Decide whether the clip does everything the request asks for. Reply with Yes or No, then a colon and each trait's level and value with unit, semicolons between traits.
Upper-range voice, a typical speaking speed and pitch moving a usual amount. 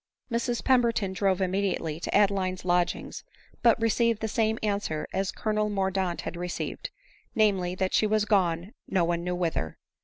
Yes: high, 195 Hz; average, 160 wpm; average, 3.2 semitones